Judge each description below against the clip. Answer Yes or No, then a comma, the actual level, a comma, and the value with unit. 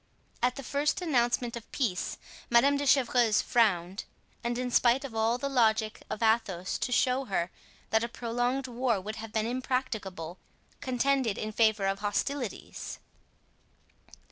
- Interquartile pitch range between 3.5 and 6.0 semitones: No, average, 2.8 semitones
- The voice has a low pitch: No, high, 235 Hz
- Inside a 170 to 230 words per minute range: No, average, 145 wpm